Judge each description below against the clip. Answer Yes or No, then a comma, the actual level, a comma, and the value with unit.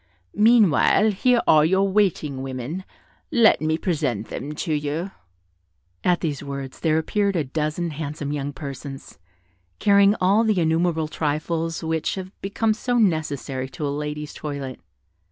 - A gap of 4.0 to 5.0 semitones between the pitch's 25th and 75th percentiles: Yes, average, 4.7 semitones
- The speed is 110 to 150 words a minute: Yes, average, 140 wpm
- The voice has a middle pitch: Yes, medium, 160 Hz